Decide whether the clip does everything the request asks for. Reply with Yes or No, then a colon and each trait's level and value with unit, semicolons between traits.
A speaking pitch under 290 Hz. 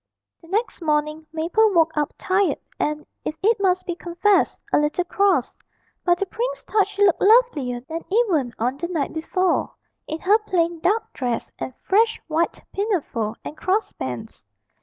No: very high, 350 Hz